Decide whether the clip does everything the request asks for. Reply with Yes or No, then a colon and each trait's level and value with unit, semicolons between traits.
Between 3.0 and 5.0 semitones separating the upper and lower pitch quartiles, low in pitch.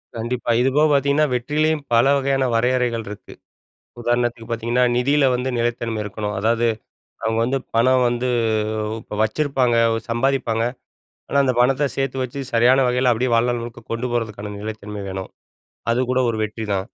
No: narrow, 2.4 semitones; low, 120 Hz